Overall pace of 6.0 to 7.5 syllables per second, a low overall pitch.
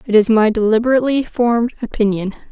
No: 6.5 syllables/s; high, 225 Hz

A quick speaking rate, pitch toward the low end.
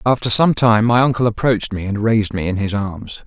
Yes: fast, 240 wpm; low, 110 Hz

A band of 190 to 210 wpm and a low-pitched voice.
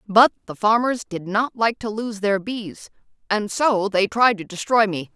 No: average, 200 wpm; high, 210 Hz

